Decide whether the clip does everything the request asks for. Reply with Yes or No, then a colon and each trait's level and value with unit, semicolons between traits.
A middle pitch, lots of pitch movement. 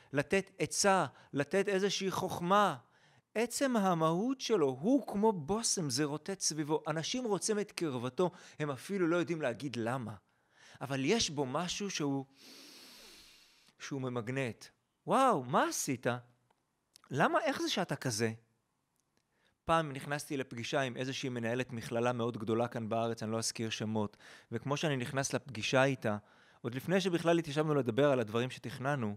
Yes: medium, 145 Hz; wide, 7.3 semitones